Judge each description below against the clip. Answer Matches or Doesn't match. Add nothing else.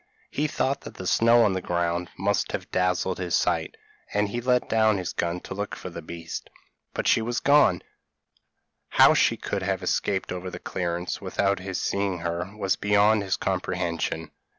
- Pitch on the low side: Matches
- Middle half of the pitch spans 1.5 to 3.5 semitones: Matches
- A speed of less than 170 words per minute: Doesn't match